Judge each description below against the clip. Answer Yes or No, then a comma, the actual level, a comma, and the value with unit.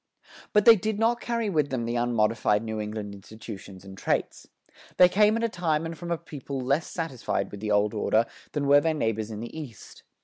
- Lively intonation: Yes, wide, 7.8 semitones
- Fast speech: Yes, fast, 210 wpm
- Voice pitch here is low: Yes, low, 130 Hz